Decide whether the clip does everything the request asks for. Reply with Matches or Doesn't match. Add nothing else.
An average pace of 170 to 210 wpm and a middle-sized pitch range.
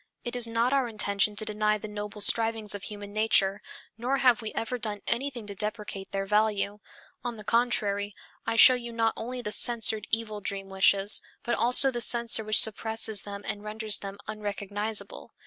Doesn't match